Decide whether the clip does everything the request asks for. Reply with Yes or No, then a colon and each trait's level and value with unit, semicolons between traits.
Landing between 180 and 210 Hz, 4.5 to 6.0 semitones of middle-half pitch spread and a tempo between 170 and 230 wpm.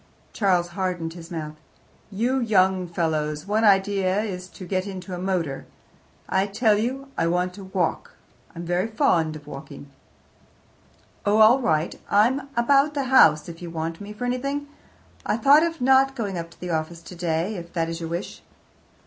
Yes: medium, 185 Hz; average, 4.9 semitones; average, 175 wpm